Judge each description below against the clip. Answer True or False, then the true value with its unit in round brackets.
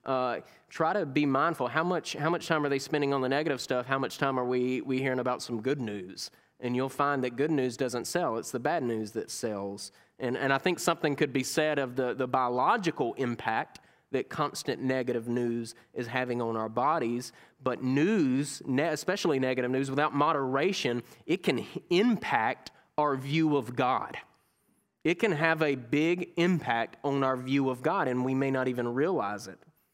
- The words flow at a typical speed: True (190 wpm)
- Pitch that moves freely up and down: False (3.1 semitones)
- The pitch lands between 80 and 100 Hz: False (135 Hz)